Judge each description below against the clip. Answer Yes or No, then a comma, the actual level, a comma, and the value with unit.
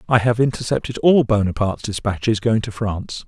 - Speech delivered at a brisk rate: No, average, 165 wpm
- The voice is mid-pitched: No, low, 110 Hz